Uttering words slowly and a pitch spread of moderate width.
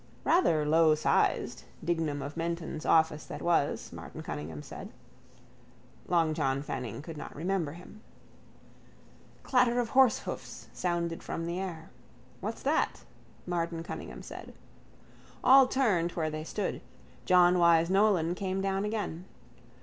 Yes: slow, 125 wpm; average, 3.4 semitones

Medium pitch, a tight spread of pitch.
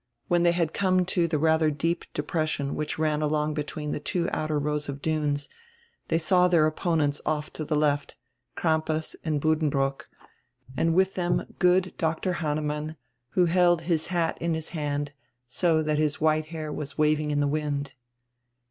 Yes: medium, 155 Hz; narrow, 1.9 semitones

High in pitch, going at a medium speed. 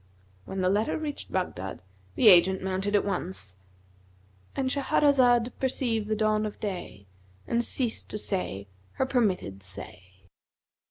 No: high, 195 Hz; slow, 125 wpm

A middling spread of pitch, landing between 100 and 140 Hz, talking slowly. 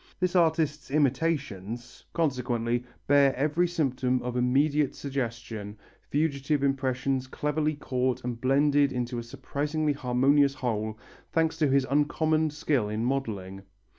Yes: average, 3.2 semitones; low, 135 Hz; slow, 120 wpm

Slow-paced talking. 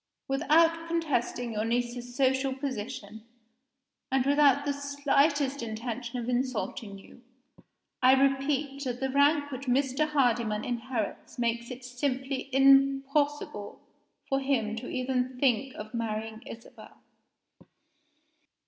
Yes: slow, 110 wpm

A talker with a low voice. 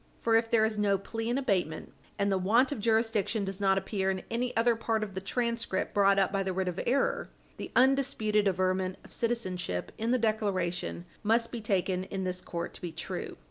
No: high, 205 Hz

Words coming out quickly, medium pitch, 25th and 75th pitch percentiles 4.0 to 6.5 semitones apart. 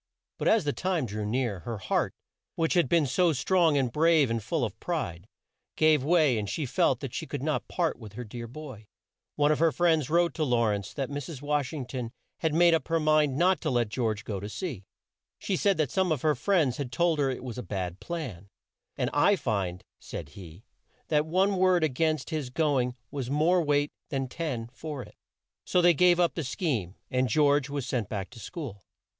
Yes: fast, 220 wpm; medium, 145 Hz; wide, 5.6 semitones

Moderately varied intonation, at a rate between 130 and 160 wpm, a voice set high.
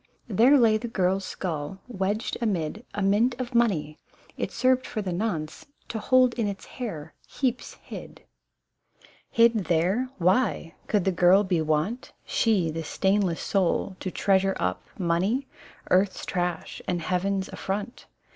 Yes: average, 4.4 semitones; average, 145 wpm; high, 195 Hz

